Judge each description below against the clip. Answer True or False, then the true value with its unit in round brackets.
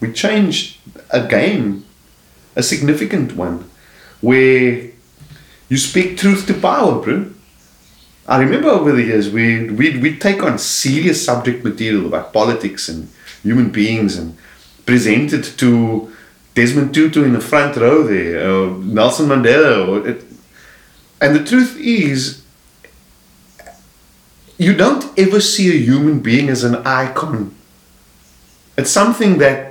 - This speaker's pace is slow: True (130 wpm)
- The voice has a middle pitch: False (125 Hz)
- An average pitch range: False (6.4 semitones)